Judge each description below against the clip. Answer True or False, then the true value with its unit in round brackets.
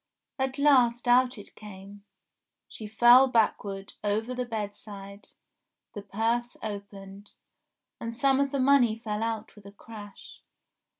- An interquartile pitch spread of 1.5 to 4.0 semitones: True (3.3 semitones)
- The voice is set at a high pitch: True (220 Hz)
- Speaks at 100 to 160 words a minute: True (135 wpm)